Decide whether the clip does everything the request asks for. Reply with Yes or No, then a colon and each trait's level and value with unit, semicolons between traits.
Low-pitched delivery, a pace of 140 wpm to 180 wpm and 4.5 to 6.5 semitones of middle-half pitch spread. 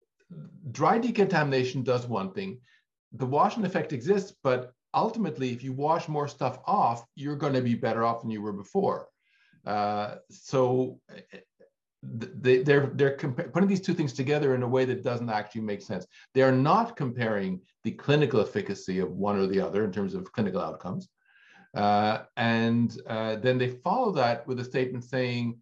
Yes: low, 130 Hz; average, 175 wpm; wide, 5.4 semitones